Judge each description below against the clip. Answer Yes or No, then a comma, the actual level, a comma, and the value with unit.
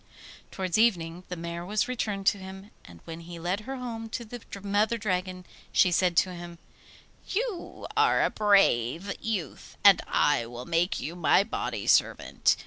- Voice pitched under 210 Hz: Yes, high, 190 Hz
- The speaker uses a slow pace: No, average, 165 wpm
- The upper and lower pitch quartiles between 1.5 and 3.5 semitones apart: No, average, 3.9 semitones